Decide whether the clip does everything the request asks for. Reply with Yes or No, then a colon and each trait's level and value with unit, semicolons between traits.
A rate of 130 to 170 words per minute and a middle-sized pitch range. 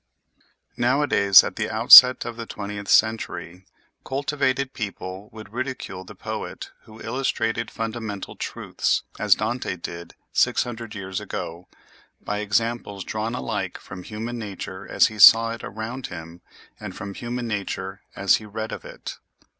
Yes: average, 145 wpm; average, 3.4 semitones